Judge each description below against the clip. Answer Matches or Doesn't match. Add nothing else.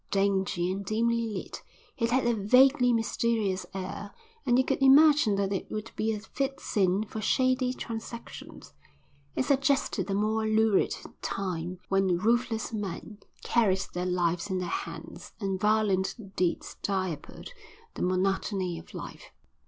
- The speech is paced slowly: Doesn't match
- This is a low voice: Doesn't match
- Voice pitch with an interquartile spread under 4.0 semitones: Matches